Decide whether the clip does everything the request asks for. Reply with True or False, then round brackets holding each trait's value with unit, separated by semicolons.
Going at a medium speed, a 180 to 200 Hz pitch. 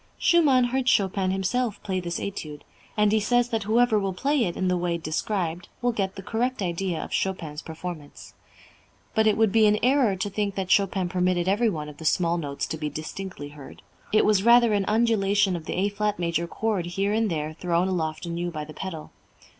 False (210 wpm; 190 Hz)